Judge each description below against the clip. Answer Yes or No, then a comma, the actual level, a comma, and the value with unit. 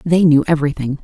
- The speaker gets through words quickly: No, average, 175 wpm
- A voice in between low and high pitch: Yes, medium, 155 Hz